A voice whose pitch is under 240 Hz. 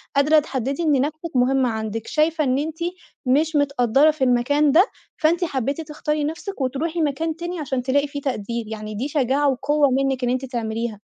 No: very high, 280 Hz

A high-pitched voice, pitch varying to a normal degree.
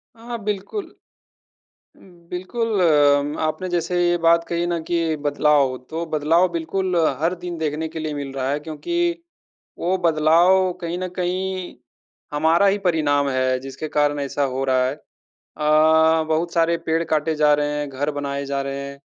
No: medium, 160 Hz; average, 3.3 semitones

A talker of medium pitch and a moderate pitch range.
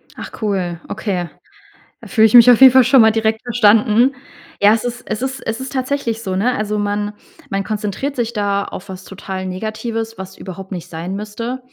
No: high, 215 Hz; average, 3.4 semitones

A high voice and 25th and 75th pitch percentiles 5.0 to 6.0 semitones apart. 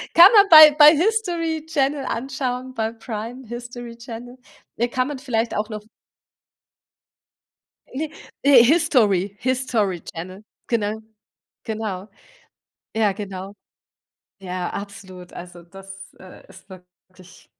Yes: high, 230 Hz; wide, 5.4 semitones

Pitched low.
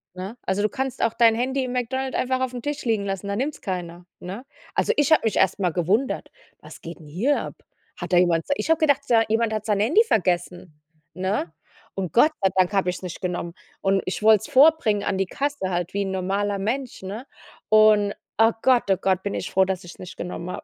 No: high, 205 Hz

